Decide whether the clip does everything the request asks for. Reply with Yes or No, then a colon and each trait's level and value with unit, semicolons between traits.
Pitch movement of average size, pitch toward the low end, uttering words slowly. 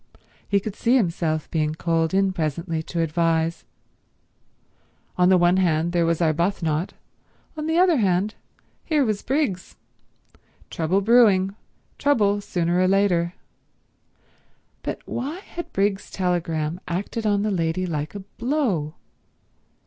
No: average, 3.8 semitones; medium, 185 Hz; slow, 125 wpm